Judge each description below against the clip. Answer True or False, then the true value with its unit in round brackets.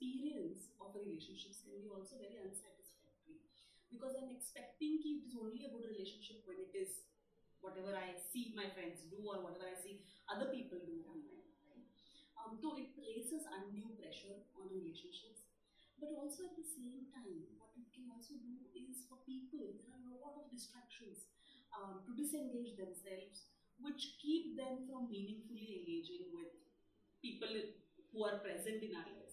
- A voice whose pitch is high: True (245 Hz)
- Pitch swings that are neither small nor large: False (6.1 semitones)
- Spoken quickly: False (170 wpm)